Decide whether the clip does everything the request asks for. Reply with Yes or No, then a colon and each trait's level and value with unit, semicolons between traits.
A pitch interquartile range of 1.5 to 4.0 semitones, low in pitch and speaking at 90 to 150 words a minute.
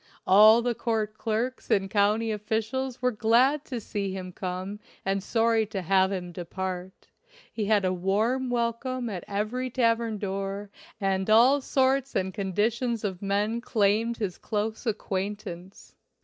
No: average, 3.3 semitones; high, 215 Hz; average, 145 wpm